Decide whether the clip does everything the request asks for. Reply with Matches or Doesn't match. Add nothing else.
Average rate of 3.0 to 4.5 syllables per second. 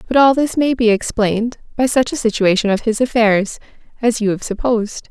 Doesn't match